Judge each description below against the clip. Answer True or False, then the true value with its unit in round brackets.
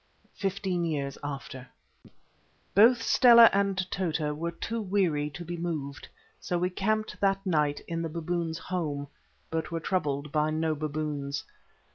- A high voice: False (165 Hz)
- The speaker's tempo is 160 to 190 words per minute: False (140 wpm)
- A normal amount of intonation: True (4.1 semitones)